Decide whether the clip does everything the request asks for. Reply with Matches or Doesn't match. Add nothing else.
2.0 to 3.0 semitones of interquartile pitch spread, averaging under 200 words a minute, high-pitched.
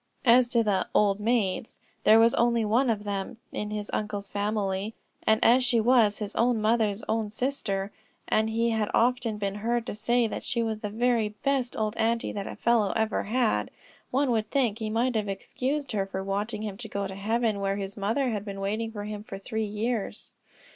Doesn't match